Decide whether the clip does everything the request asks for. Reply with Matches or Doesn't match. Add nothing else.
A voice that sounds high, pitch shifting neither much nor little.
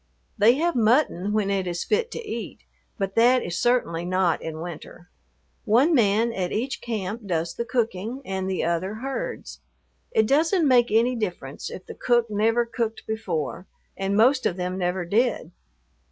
Matches